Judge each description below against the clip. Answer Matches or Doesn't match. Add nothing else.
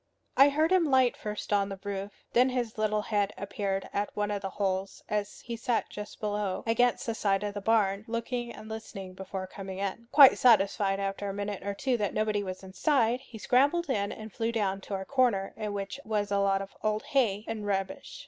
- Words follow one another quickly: Matches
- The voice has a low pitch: Doesn't match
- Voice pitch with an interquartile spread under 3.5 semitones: Matches